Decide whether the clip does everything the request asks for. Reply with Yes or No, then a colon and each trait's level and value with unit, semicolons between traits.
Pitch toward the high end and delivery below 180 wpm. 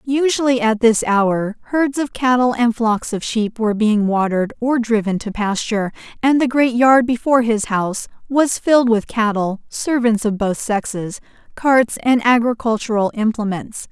Yes: high, 230 Hz; average, 160 wpm